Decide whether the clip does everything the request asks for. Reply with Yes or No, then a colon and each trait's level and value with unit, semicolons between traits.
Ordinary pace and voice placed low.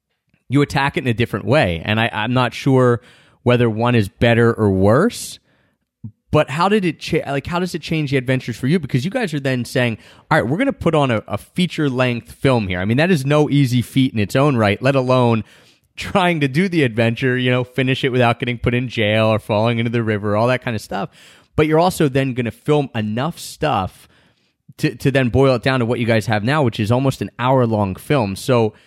No: fast, 245 wpm; low, 125 Hz